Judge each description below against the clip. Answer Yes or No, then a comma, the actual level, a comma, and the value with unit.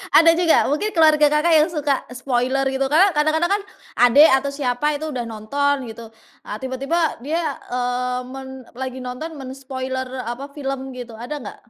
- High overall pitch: Yes, very high, 270 Hz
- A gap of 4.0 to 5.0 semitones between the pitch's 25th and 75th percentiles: No, average, 3.3 semitones